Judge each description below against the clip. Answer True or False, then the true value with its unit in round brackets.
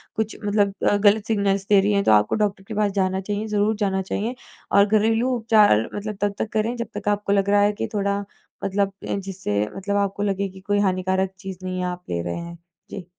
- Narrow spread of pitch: True (1.5 semitones)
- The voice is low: False (200 Hz)